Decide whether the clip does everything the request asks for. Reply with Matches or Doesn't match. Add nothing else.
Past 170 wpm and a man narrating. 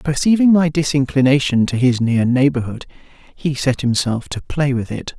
Doesn't match